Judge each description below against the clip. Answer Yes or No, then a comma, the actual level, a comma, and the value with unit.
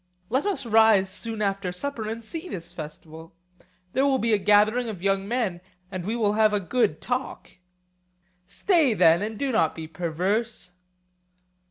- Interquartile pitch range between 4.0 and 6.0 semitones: Yes, average, 4.6 semitones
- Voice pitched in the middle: No, high, 210 Hz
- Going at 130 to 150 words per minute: No, average, 165 wpm